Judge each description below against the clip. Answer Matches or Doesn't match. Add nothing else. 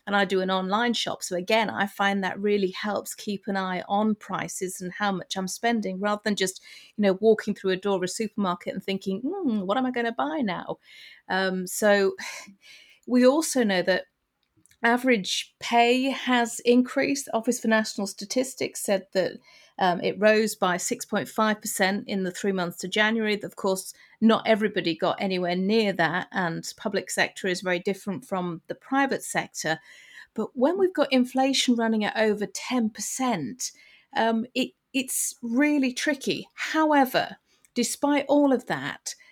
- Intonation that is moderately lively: Matches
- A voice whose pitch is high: Matches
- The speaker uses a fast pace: Doesn't match